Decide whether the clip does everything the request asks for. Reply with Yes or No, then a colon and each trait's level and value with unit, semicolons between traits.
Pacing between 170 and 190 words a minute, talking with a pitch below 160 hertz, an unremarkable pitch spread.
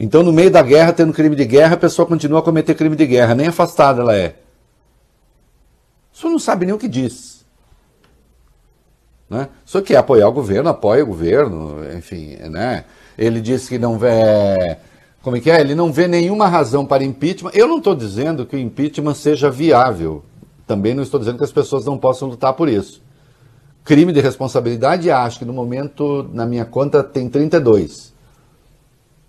Yes: fast, 185 wpm; medium, 140 Hz; average, 4.7 semitones